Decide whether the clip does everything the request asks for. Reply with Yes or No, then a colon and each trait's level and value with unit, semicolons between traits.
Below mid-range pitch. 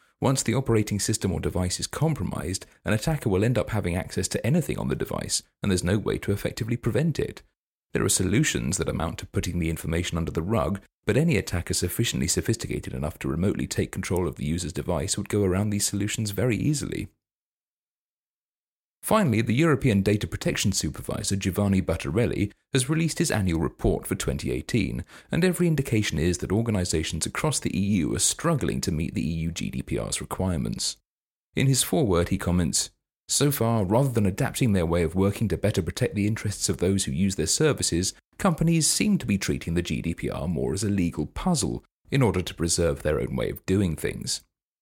Yes: low, 100 Hz